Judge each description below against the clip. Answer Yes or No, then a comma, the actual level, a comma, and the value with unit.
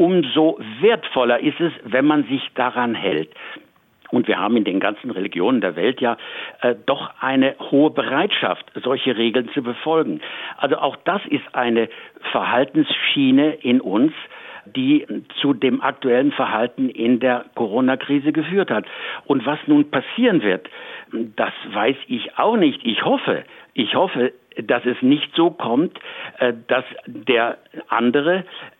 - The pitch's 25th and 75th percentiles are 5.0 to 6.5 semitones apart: Yes, wide, 5.6 semitones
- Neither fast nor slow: Yes, average, 145 wpm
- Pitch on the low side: No, medium, 145 Hz